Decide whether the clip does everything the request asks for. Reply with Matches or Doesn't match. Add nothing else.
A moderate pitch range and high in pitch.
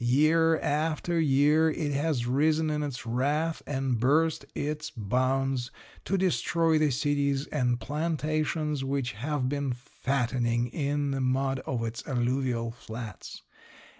Doesn't match